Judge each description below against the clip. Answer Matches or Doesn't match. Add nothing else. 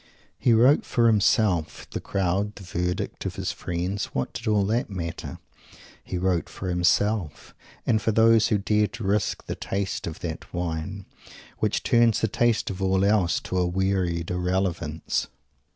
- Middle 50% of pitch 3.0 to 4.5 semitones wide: Matches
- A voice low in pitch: Matches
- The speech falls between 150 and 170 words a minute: Matches